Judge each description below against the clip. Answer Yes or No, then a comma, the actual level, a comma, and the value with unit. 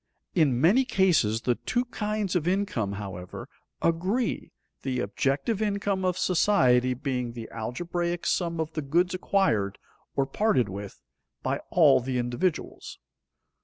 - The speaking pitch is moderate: Yes, medium, 160 Hz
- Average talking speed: No, slow, 130 wpm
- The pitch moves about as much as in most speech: No, wide, 7.5 semitones